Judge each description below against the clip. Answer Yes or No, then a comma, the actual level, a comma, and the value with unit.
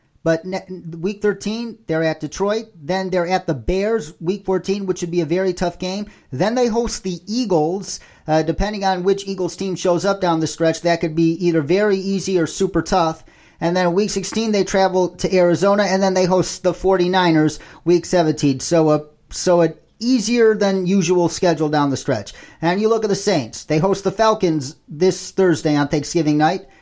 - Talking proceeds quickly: No, average, 195 wpm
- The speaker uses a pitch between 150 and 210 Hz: Yes, medium, 185 Hz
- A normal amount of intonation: Yes, average, 3.0 semitones